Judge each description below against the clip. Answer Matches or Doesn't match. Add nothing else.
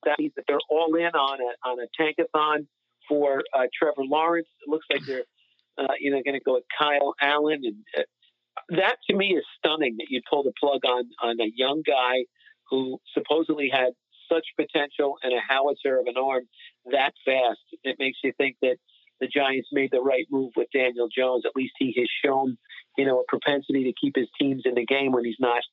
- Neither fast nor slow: Doesn't match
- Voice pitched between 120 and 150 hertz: Matches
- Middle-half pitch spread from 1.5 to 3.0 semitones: Doesn't match